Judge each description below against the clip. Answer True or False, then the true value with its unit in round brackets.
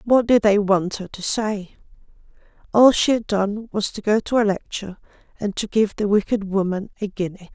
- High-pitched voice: True (205 Hz)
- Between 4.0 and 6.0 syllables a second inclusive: True (5.1 syllables/s)